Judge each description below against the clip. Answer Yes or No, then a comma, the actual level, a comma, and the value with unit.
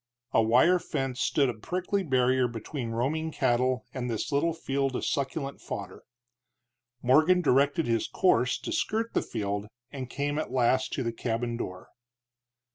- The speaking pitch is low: Yes, low, 130 Hz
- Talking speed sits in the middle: Yes, average, 155 wpm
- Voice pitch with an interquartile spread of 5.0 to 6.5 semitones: No, average, 4.3 semitones